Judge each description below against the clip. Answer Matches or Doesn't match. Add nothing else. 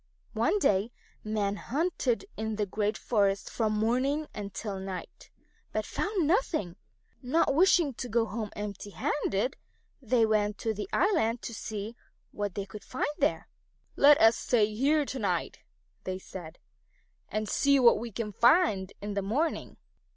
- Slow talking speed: Doesn't match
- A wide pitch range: Doesn't match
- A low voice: Doesn't match